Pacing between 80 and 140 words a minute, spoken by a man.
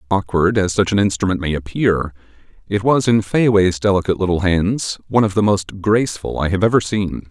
No: average, 190 wpm; male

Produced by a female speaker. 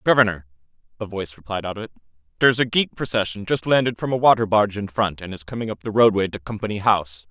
No: male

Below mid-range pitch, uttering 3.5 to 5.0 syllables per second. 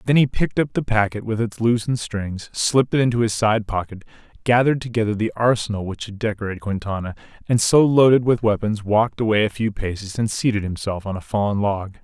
No: low, 110 Hz; 6.0 syllables/s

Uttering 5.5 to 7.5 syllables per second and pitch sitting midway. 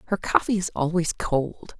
No: 4.6 syllables/s; medium, 170 Hz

